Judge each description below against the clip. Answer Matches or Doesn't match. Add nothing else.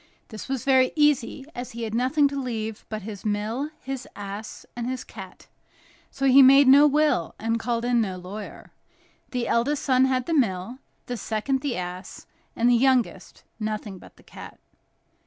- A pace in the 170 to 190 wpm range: Matches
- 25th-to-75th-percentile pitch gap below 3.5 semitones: Doesn't match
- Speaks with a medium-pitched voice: Doesn't match